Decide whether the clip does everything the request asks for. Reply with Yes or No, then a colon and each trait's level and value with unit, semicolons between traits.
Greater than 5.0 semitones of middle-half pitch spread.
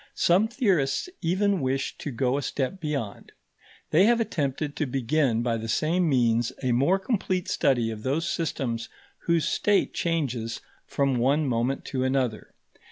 Yes: wide, 5.4 semitones